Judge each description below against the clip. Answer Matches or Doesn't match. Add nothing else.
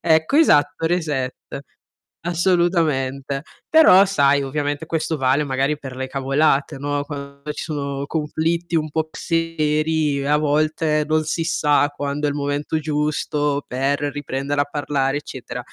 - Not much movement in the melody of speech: Matches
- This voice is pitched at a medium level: Matches